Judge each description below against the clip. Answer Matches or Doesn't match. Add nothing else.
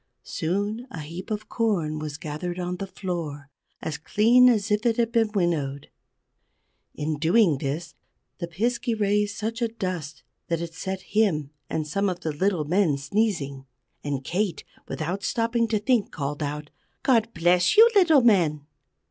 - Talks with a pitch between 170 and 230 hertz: Matches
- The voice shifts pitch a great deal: Matches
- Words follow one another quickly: Doesn't match